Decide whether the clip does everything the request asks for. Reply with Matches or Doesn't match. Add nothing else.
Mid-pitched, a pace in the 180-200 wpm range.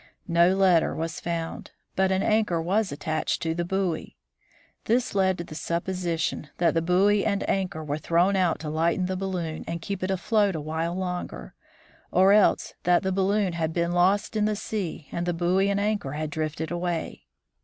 Matches